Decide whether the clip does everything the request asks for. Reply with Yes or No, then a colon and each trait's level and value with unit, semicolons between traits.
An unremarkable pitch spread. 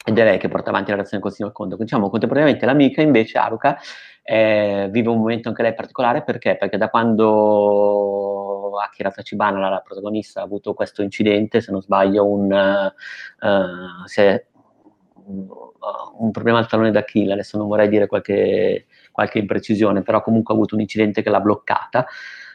No: narrow, 1.7 semitones